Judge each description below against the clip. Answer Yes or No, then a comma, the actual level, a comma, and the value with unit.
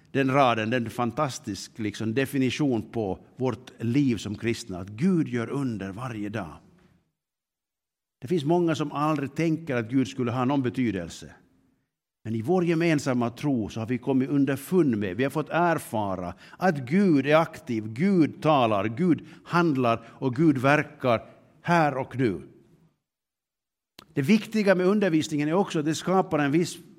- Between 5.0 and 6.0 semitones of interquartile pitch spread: Yes, wide, 5.4 semitones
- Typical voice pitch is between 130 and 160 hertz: Yes, low, 135 Hz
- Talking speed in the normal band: Yes, average, 155 wpm